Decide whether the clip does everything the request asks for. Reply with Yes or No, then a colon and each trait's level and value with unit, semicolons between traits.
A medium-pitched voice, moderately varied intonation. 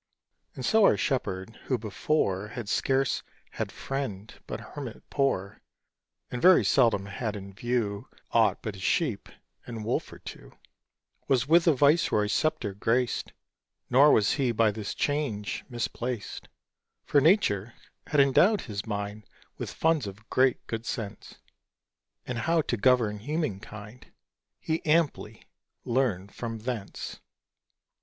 No: low, 120 Hz; average, 4.9 semitones